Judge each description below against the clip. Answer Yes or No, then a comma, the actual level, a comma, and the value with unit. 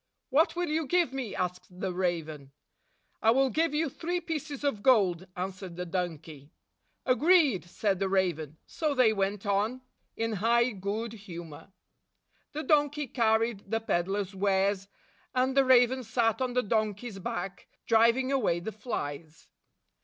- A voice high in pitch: Yes, high, 220 Hz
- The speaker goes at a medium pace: Yes, average, 155 wpm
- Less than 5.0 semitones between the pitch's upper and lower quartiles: No, wide, 5.6 semitones